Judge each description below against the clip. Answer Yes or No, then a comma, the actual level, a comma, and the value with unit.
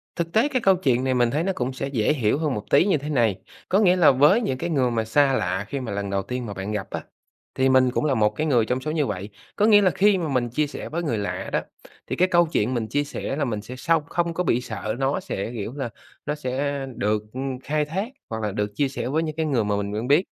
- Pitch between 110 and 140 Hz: Yes, low, 135 Hz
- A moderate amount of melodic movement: No, wide, 5.7 semitones